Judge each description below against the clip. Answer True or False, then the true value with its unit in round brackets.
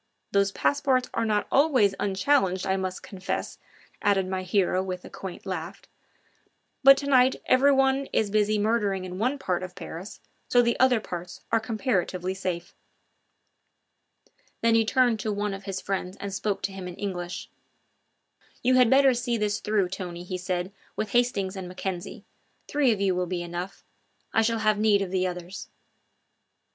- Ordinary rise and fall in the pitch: True (3.9 semitones)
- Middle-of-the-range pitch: False (200 Hz)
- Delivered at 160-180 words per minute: True (170 wpm)